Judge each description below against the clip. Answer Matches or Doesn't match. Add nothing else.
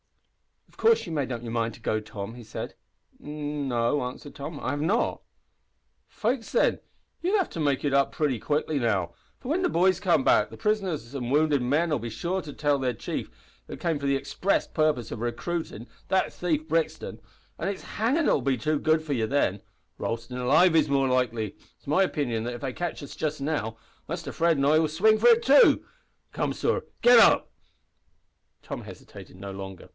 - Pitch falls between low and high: Matches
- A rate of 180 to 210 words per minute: Matches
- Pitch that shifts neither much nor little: Doesn't match